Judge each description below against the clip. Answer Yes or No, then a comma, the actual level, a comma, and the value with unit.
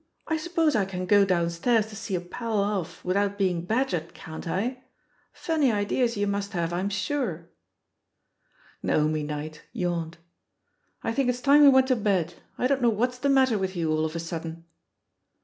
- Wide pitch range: Yes, wide, 6.5 semitones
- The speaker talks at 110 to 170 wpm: No, average, 180 wpm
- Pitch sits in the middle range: No, high, 200 Hz